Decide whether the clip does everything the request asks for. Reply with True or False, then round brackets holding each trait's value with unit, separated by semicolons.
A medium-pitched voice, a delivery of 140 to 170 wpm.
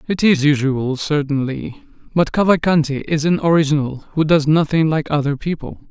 True (150 Hz; 150 wpm)